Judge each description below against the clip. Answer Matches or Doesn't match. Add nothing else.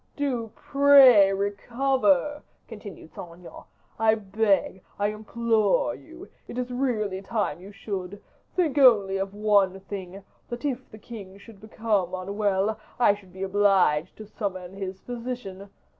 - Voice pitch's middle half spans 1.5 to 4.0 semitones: Matches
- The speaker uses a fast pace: Doesn't match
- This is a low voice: Doesn't match